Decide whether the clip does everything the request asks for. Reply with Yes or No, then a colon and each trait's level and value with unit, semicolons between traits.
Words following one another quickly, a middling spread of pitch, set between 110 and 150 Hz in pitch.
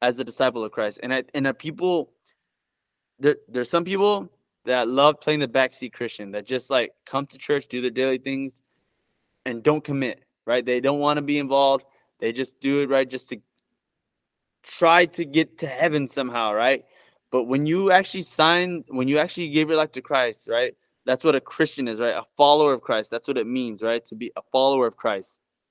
Yes: fast, 210 wpm; average, 3.1 semitones; low, 135 Hz